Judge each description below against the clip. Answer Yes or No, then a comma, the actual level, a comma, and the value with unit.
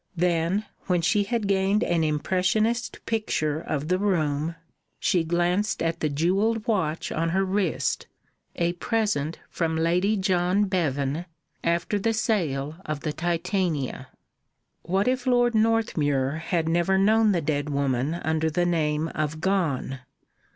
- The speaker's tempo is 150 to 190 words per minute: No, slow, 135 wpm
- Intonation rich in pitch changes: No, average, 4.4 semitones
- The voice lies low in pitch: No, medium, 175 Hz